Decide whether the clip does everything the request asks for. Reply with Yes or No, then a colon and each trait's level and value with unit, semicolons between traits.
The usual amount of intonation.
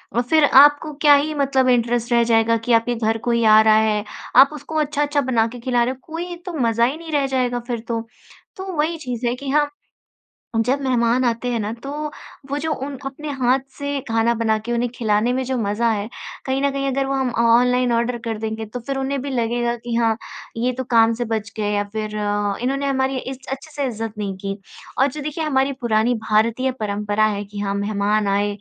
Yes: average, 3.4 semitones